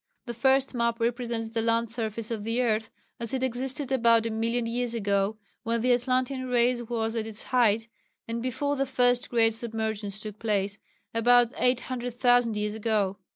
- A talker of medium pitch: No, high, 230 Hz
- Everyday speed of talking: Yes, average, 170 wpm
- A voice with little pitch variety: Yes, narrow, 1.8 semitones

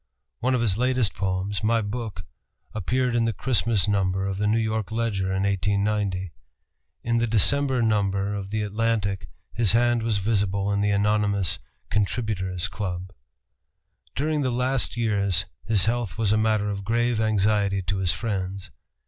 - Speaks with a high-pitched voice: No, low, 105 Hz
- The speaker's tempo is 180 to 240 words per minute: No, average, 155 wpm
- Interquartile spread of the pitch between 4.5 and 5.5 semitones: No, average, 2.8 semitones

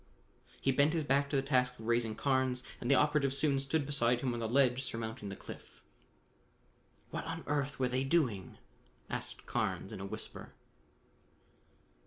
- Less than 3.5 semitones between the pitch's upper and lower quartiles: Yes, average, 3.0 semitones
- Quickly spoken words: No, average, 170 wpm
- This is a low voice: Yes, low, 130 Hz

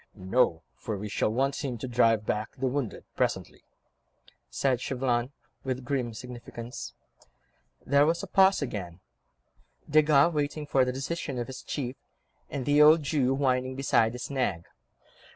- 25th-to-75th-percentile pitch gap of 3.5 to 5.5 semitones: No, average, 3.1 semitones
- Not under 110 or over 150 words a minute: Yes, average, 145 wpm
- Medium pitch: No, low, 130 Hz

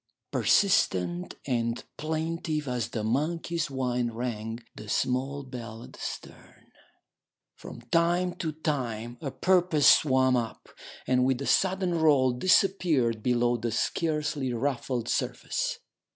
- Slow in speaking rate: Yes, slow, 125 wpm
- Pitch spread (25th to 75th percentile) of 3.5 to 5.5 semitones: Yes, average, 5.1 semitones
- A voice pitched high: No, low, 130 Hz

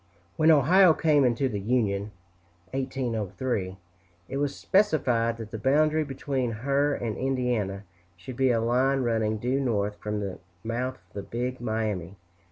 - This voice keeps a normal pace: Yes, average, 150 wpm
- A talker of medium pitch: No, low, 120 Hz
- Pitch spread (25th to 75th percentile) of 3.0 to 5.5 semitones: Yes, average, 4.0 semitones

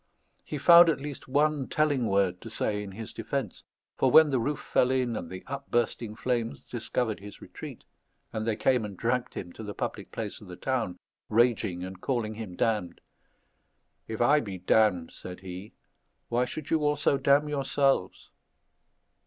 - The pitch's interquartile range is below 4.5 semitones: No, average, 4.9 semitones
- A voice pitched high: No, low, 115 Hz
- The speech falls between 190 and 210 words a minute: No, average, 170 wpm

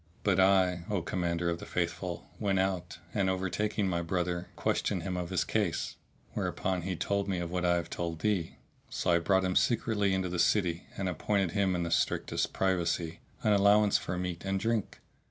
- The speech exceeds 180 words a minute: Yes, average, 190 wpm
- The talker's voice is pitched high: No, very low, 95 Hz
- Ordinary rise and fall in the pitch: No, narrow, 2.2 semitones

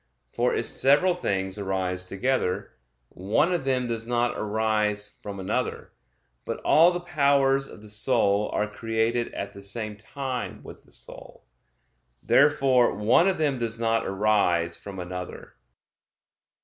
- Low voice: Yes, low, 110 Hz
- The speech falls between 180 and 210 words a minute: No, average, 140 wpm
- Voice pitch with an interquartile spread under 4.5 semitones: No, average, 5.0 semitones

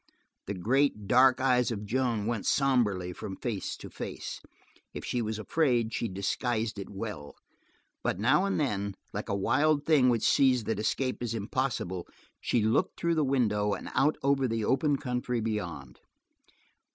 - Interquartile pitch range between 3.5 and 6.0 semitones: Yes, average, 4.2 semitones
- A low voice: Yes, low, 115 Hz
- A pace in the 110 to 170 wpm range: Yes, average, 165 wpm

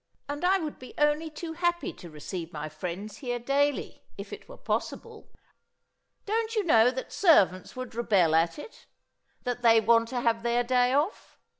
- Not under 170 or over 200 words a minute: Yes, average, 175 wpm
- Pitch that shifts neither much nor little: No, wide, 5.9 semitones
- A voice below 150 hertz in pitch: No, high, 245 Hz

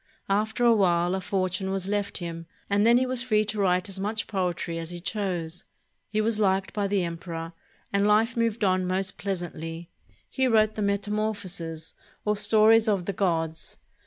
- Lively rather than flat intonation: No, average, 3.3 semitones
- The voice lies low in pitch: No, high, 195 Hz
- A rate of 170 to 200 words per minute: Yes, average, 180 wpm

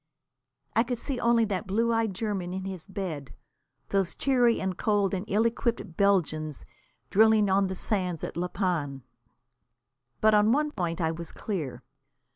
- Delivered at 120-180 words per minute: Yes, average, 160 wpm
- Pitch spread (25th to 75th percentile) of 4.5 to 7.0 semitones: No, average, 4.0 semitones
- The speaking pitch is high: Yes, high, 195 Hz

